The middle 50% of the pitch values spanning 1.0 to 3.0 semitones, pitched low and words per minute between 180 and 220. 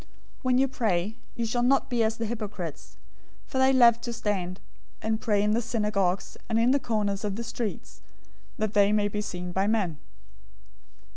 No: average, 2.7 semitones; high, 215 Hz; average, 190 wpm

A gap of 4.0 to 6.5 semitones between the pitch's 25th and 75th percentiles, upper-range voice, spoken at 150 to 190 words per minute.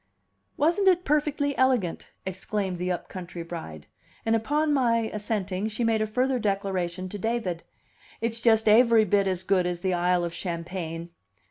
Yes: average, 4.6 semitones; high, 205 Hz; average, 160 wpm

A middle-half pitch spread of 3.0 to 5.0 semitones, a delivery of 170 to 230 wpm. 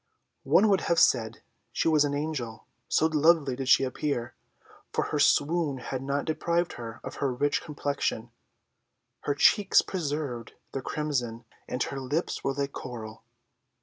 No: average, 3.7 semitones; average, 150 wpm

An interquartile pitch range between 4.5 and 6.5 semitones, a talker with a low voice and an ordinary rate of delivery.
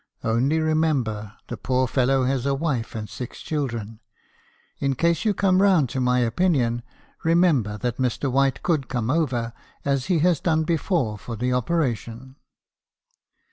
Yes: average, 5.0 semitones; low, 130 Hz; average, 150 wpm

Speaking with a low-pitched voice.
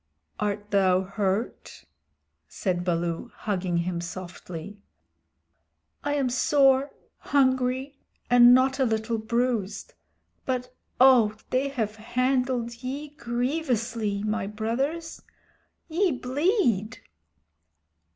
No: high, 240 Hz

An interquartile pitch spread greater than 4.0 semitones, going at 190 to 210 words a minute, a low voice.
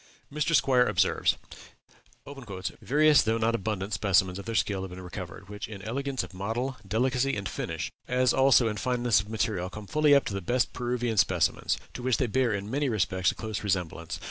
Yes: average, 4.6 semitones; average, 195 wpm; low, 110 Hz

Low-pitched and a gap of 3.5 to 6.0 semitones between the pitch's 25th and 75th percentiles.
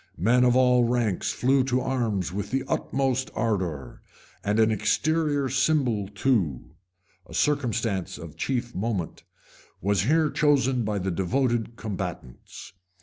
Yes: low, 120 Hz; average, 5.1 semitones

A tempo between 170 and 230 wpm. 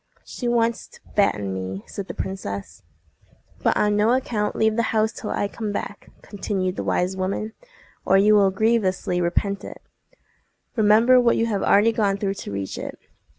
Yes: average, 175 wpm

